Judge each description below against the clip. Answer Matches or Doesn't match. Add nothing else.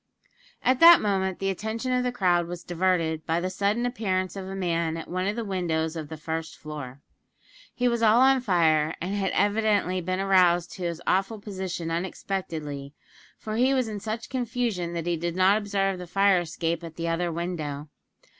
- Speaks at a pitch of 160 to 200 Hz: Matches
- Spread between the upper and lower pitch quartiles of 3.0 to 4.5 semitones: Matches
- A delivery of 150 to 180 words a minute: Doesn't match